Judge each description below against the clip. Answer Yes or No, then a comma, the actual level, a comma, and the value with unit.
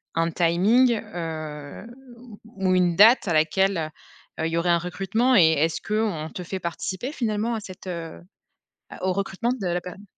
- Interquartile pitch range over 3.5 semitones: Yes, average, 4.0 semitones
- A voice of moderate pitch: Yes, medium, 180 Hz